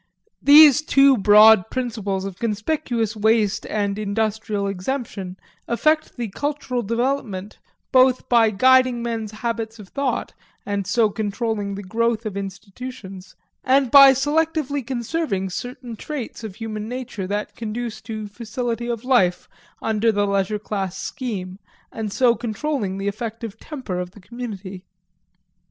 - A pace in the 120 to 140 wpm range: Yes, slow, 135 wpm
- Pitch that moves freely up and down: No, average, 3.8 semitones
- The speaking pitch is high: Yes, high, 225 Hz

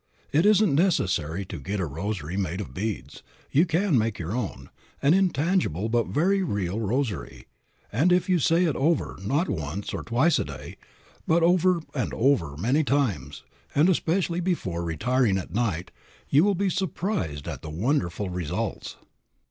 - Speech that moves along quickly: No, average, 165 wpm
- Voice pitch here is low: Yes, low, 120 Hz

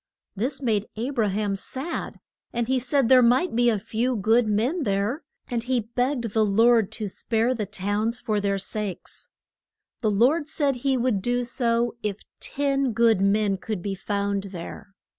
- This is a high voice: Yes, high, 230 Hz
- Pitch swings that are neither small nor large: Yes, average, 3.5 semitones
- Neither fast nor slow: Yes, average, 175 wpm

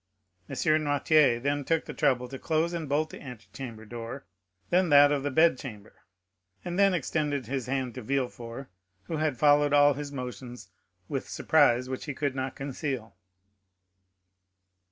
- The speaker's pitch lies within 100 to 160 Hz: Yes, medium, 140 Hz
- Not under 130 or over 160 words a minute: Yes, average, 155 wpm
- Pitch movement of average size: Yes, average, 3.0 semitones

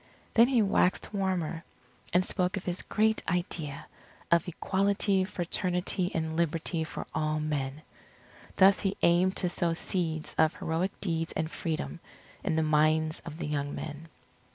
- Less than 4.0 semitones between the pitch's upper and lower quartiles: Yes, average, 3.0 semitones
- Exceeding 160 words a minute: No, average, 150 wpm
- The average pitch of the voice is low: No, medium, 170 Hz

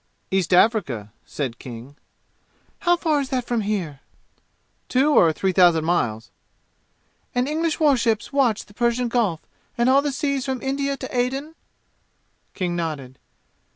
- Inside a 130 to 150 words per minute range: Yes, average, 145 wpm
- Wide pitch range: Yes, wide, 8.2 semitones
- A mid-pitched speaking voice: No, high, 235 Hz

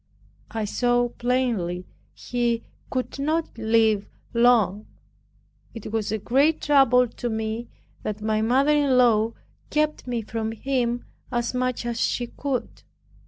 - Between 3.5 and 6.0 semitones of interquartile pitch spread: No, narrow, 2.4 semitones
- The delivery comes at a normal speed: No, slow, 130 wpm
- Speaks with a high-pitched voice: Yes, high, 240 Hz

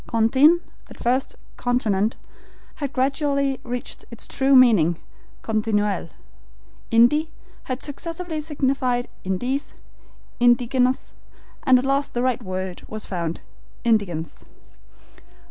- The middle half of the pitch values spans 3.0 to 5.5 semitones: Yes, average, 4.0 semitones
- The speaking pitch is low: No, high, 245 Hz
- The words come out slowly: Yes, slow, 100 wpm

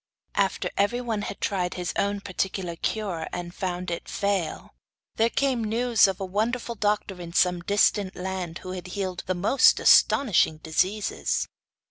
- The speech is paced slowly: No, average, 150 wpm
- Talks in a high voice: Yes, high, 195 Hz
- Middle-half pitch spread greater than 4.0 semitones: No, average, 2.9 semitones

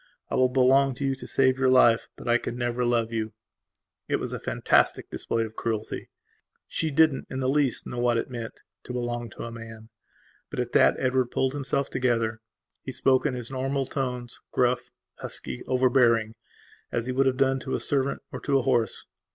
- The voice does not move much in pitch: Yes, narrow, 2.1 semitones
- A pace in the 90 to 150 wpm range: No, average, 195 wpm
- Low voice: Yes, low, 125 Hz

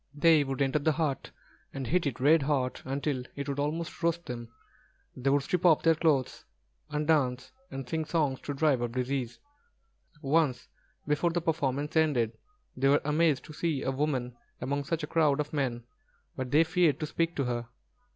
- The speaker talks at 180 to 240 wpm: Yes, average, 185 wpm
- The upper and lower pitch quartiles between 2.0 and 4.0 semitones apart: Yes, average, 3.1 semitones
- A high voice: No, medium, 145 Hz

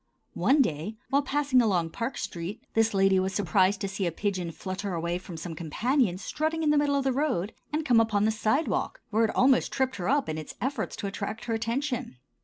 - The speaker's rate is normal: No, fast, 215 wpm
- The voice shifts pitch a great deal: Yes, wide, 6.1 semitones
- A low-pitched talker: No, high, 215 Hz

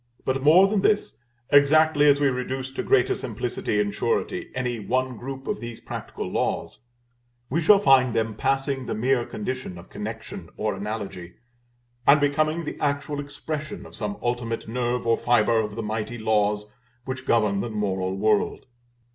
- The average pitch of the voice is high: No, low, 125 Hz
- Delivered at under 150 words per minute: No, average, 165 wpm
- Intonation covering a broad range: No, average, 4.9 semitones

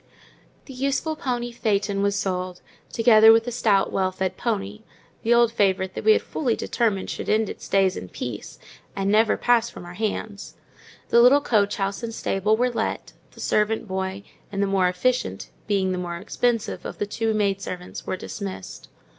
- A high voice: Yes, high, 205 Hz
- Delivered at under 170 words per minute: No, average, 180 wpm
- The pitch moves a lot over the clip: No, average, 3.3 semitones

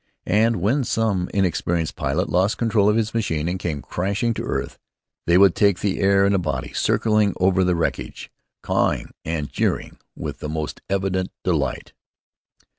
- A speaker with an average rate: Yes, average, 165 wpm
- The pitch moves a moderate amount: Yes, average, 3.2 semitones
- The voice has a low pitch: Yes, very low, 95 Hz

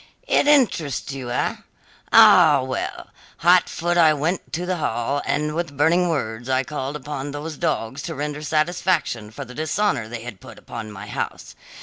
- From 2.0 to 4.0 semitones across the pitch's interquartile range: No, average, 4.7 semitones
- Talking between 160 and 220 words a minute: Yes, average, 170 wpm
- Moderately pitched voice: Yes, medium, 145 Hz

